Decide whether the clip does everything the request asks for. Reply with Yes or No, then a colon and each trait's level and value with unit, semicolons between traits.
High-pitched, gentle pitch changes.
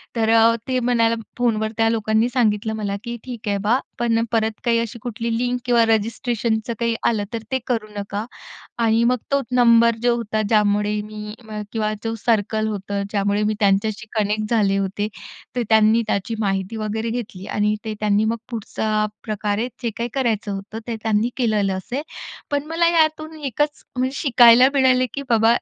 Yes: high, 225 Hz; narrow, 2.1 semitones